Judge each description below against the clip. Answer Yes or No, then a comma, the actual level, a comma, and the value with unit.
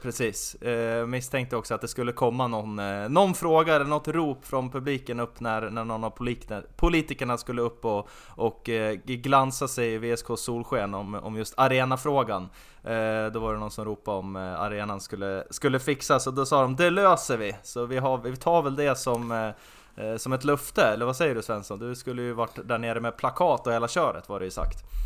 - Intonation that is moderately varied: Yes, average, 3.4 semitones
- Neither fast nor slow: No, fast, 200 wpm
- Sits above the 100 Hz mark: Yes, low, 120 Hz